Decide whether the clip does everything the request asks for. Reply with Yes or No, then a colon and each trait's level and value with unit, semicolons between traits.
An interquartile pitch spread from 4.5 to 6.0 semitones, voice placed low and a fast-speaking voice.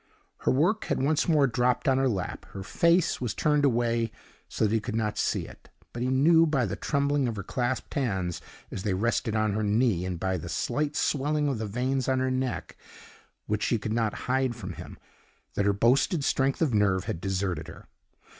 Yes: average, 4.8 semitones; low, 120 Hz; fast, 210 wpm